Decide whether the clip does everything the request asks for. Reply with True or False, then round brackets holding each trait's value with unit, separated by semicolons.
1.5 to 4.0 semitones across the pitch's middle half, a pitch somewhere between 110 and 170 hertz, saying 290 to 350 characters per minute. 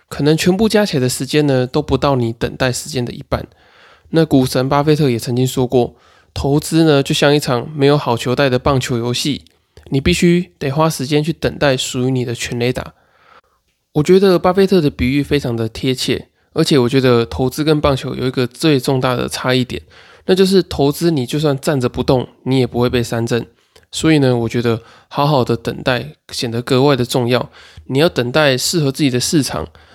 True (3.4 semitones; 135 Hz; 300 characters per minute)